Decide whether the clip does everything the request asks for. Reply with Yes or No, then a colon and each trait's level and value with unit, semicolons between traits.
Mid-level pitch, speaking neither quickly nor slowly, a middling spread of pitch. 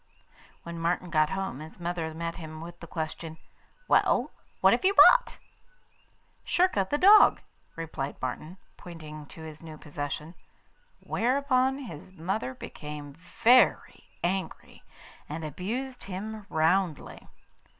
No: medium, 170 Hz; slow, 120 wpm; average, 4.5 semitones